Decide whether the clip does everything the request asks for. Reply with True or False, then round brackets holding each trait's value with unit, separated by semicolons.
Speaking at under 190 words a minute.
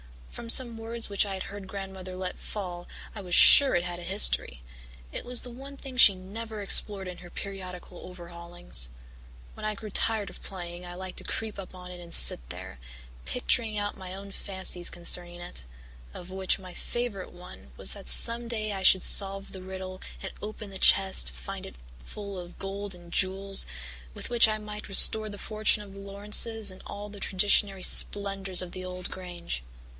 False (195 wpm)